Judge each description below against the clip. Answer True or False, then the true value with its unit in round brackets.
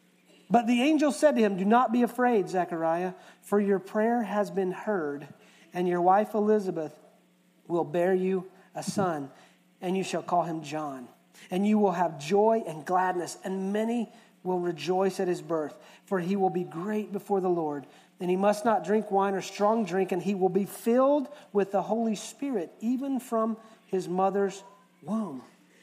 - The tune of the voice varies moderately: True (3.1 semitones)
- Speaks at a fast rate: False (180 wpm)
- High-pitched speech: True (195 Hz)